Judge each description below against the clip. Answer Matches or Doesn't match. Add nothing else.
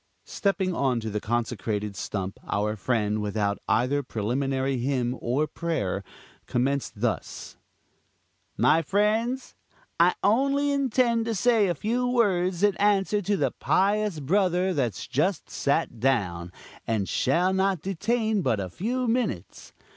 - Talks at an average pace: Doesn't match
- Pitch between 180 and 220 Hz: Doesn't match